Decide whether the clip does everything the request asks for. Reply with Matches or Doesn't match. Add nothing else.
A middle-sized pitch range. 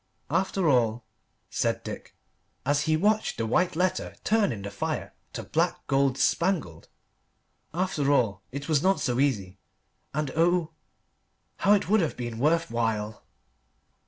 Doesn't match